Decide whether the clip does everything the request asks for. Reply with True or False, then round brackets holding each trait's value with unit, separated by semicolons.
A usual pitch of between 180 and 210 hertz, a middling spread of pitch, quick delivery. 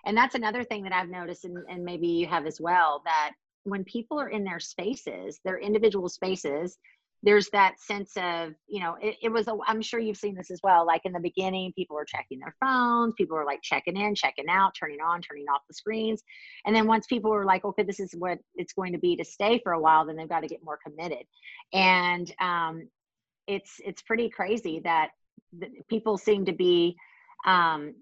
True (185 Hz; 3.8 semitones; 220 wpm)